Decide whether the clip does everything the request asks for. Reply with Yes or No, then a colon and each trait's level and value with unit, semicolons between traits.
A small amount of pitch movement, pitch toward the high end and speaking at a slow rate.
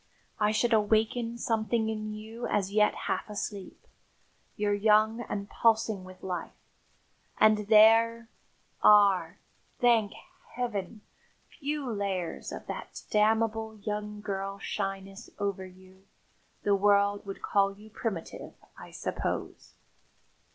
Yes: narrow, 1.9 semitones; high, 210 Hz; slow, 115 wpm